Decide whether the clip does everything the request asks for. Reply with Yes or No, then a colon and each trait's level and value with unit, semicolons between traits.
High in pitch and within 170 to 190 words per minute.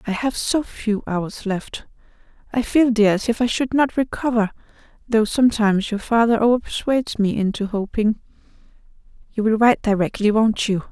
No: high, 220 Hz; average, 160 wpm